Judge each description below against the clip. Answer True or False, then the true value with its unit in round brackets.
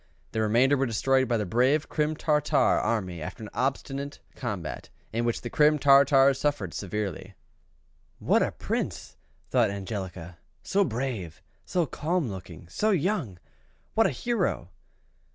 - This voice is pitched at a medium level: False (130 Hz)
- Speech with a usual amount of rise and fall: False (6.0 semitones)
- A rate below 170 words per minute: True (140 wpm)